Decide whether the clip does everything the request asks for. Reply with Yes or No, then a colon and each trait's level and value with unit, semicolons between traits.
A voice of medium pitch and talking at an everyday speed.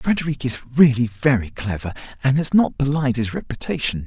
No: low, 125 Hz; average, 160 wpm